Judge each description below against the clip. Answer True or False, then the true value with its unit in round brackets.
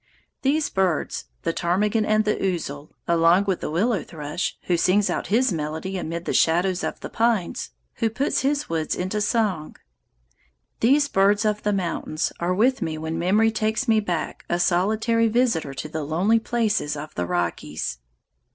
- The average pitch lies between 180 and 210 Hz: True (190 Hz)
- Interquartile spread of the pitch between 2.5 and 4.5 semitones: False (5.2 semitones)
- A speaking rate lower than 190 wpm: True (170 wpm)